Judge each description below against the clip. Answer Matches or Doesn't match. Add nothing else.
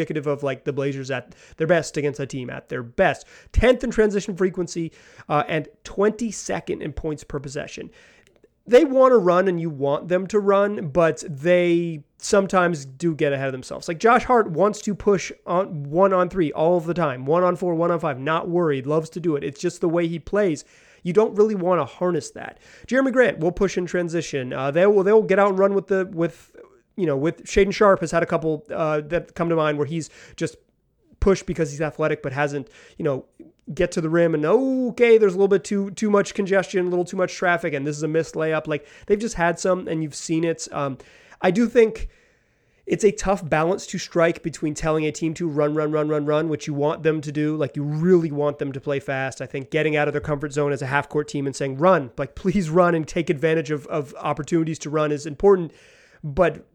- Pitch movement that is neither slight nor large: Matches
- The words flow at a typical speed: Doesn't match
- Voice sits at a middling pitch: Matches